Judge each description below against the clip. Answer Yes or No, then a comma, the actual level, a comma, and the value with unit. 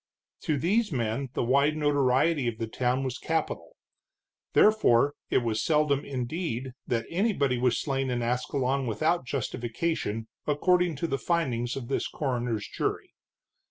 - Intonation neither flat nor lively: Yes, average, 4.2 semitones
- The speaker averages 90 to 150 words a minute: Yes, average, 140 wpm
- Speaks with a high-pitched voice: No, low, 135 Hz